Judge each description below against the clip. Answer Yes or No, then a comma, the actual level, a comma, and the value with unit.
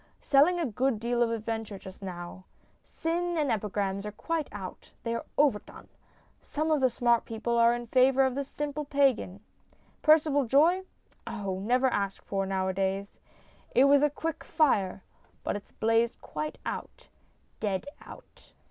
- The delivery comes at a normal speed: Yes, average, 155 wpm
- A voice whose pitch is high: Yes, high, 235 Hz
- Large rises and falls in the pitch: Yes, wide, 6.0 semitones